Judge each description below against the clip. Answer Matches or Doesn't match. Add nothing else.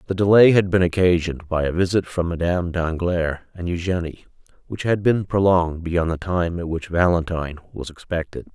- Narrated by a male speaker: Matches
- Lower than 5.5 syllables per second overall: Doesn't match